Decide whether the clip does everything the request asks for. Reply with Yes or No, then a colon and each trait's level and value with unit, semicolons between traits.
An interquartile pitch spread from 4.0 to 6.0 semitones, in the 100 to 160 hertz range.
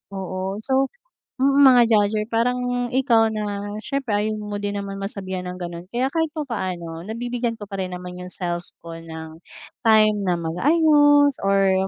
No: average, 5.2 semitones; high, 205 Hz